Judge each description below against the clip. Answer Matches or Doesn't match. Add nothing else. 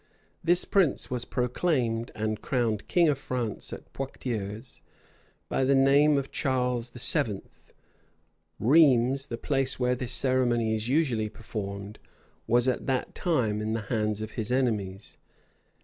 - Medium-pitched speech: Doesn't match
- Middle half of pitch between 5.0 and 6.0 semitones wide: Doesn't match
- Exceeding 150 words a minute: Doesn't match